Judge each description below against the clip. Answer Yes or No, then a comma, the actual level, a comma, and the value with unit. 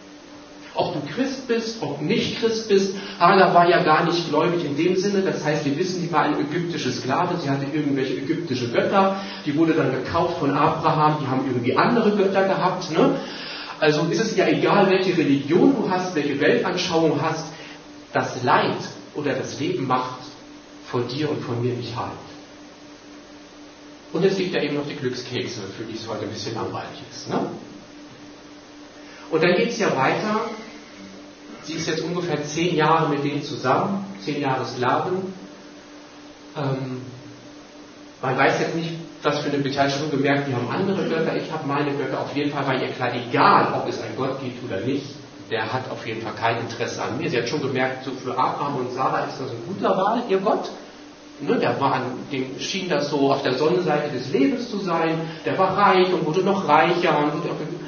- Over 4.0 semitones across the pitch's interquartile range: Yes, average, 4.9 semitones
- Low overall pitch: No, medium, 150 Hz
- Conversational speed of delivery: No, fast, 195 wpm